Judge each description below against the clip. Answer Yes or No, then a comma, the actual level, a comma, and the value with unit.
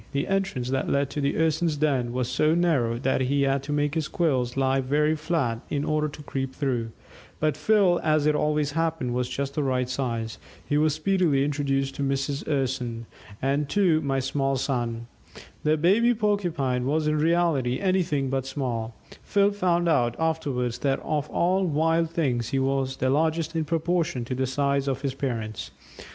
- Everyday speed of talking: Yes, average, 180 wpm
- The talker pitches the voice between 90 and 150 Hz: Yes, medium, 140 Hz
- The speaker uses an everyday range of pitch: Yes, average, 3.4 semitones